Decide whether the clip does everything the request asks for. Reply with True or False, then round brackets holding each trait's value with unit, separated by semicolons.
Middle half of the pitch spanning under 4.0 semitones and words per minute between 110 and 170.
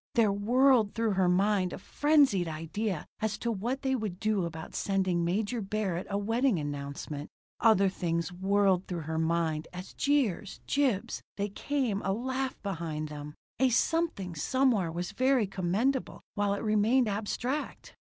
False (5.2 semitones; 150 wpm)